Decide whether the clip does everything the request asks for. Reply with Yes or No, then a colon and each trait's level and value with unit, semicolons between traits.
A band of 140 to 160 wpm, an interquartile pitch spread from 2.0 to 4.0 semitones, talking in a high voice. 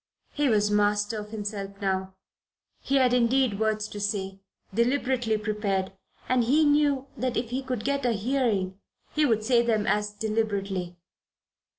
Yes: average, 155 wpm; average, 3.5 semitones; high, 220 Hz